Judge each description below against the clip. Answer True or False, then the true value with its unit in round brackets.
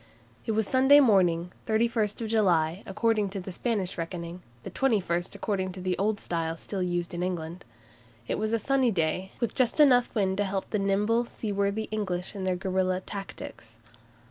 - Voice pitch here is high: True (195 Hz)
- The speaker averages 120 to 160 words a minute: False (175 wpm)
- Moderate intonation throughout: True (3.5 semitones)